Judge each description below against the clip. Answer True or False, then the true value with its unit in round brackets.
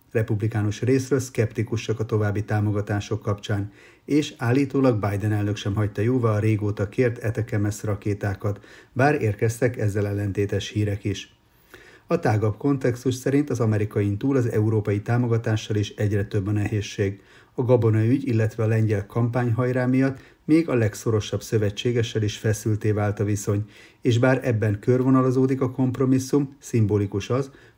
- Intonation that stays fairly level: False (3.4 semitones)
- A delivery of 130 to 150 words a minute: True (140 wpm)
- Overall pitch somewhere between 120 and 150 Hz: False (110 Hz)